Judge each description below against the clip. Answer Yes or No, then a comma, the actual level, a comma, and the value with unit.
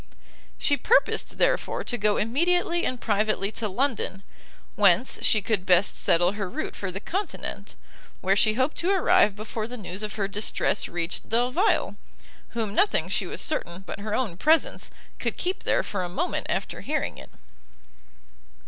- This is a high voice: Yes, high, 215 Hz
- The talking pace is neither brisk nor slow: Yes, average, 165 wpm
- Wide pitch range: Yes, wide, 6.0 semitones